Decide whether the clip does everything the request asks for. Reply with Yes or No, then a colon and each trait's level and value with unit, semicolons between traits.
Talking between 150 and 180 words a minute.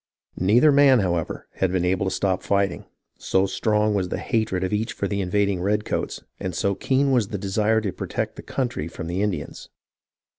No: average, 190 wpm